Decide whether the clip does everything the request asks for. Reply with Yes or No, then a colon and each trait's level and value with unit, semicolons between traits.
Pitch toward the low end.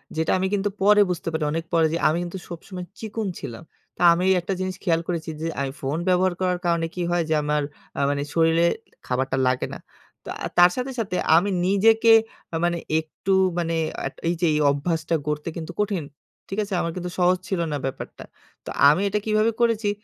No: medium, 175 Hz